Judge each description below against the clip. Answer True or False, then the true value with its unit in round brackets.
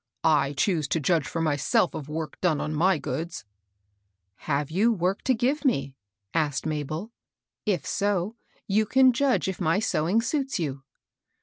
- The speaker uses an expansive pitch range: True (5.8 semitones)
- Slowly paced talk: False (170 wpm)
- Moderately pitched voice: True (165 Hz)